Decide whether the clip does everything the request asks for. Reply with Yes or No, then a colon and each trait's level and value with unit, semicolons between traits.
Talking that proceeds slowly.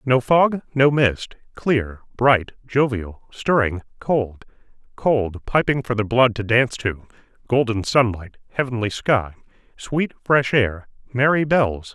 Yes: slow, 130 wpm